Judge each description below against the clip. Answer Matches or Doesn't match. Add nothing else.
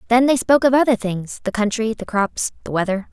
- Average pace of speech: Doesn't match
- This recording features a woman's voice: Matches